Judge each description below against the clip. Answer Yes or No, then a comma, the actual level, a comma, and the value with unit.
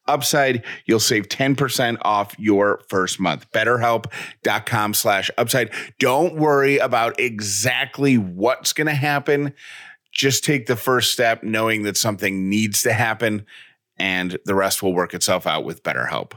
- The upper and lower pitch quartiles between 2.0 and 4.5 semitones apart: No, average, 5.0 semitones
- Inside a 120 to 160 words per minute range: Yes, average, 145 wpm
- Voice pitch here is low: Yes, low, 115 Hz